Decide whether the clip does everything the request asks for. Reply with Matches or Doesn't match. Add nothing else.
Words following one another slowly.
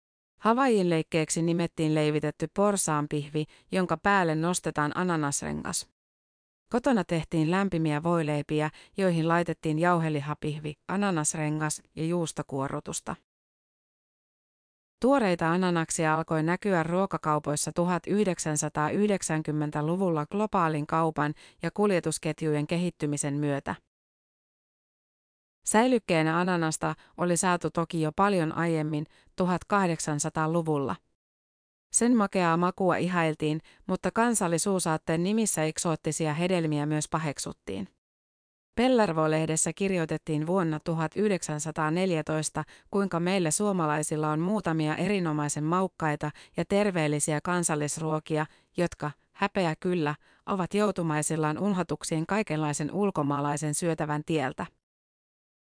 Matches